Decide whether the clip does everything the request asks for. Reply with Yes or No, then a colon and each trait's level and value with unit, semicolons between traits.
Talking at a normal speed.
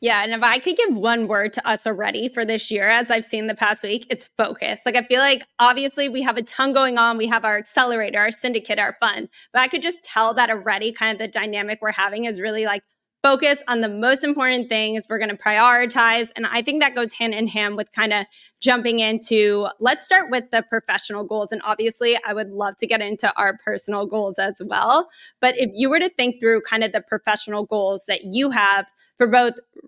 No: fast, 235 wpm